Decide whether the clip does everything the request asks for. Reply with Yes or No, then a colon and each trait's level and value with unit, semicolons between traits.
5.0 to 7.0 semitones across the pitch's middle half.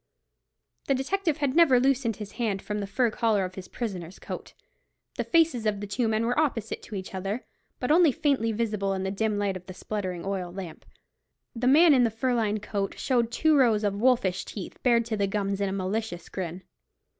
No: average, 4.2 semitones